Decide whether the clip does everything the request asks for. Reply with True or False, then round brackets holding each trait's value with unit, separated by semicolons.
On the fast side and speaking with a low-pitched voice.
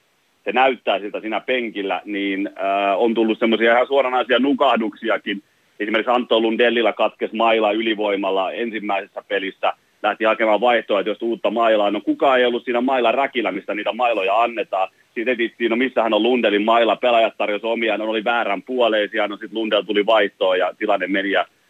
True (170 wpm; 110 Hz)